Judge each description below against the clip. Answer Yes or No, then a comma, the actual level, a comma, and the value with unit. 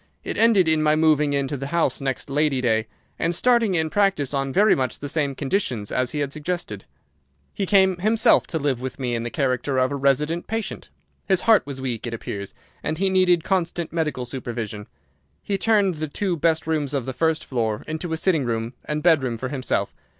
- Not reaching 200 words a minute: No, fast, 205 wpm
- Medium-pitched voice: Yes, medium, 150 Hz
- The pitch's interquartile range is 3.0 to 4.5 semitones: No, average, 5.0 semitones